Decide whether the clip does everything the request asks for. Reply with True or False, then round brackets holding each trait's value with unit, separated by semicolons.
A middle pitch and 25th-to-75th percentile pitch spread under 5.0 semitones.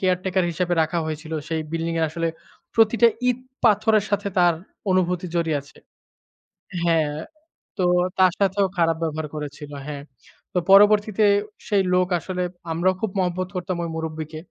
True (180 Hz; 3.0 semitones)